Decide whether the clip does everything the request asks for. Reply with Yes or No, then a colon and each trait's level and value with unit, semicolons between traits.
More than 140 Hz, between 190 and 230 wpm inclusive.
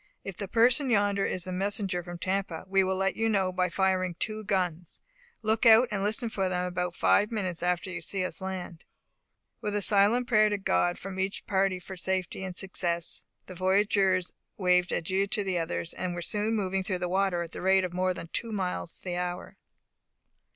Yes: high, 190 Hz; average, 200 wpm